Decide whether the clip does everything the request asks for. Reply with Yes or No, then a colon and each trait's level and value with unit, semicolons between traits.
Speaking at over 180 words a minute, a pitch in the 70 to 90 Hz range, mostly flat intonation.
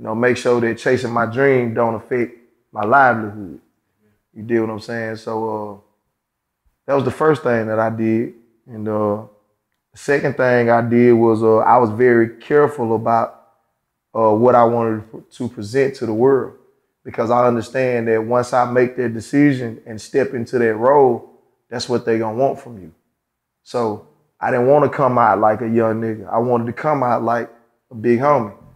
No: average, 190 wpm; low, 115 Hz; narrow, 2.0 semitones